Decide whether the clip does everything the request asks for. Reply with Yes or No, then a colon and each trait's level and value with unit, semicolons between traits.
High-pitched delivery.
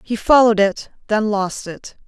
Yes: high, 210 Hz